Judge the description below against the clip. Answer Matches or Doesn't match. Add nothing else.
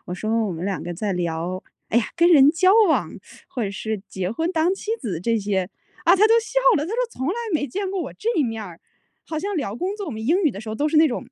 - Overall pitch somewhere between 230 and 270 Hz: Matches